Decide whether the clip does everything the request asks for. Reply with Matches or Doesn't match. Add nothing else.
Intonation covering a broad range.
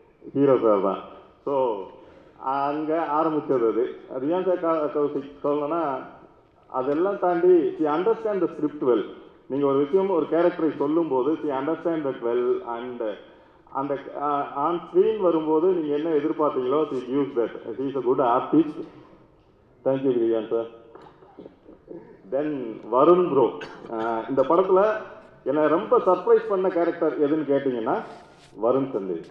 Matches